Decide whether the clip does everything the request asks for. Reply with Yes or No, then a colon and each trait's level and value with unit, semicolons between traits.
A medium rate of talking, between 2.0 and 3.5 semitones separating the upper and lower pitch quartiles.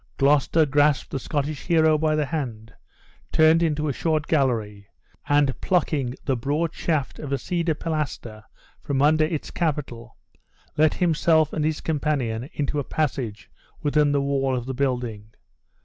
Yes: average, 150 wpm; average, 3.1 semitones